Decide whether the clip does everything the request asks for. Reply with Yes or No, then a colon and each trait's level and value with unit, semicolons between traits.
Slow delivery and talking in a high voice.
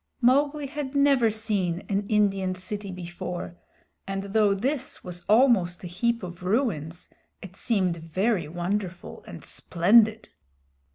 Yes: slow, 125 wpm; high, 200 Hz